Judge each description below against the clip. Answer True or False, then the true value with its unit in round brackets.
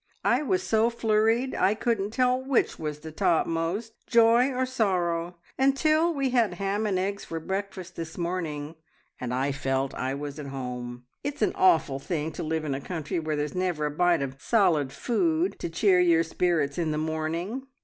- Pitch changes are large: True (6.7 semitones)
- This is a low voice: False (175 Hz)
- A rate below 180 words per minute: False (185 wpm)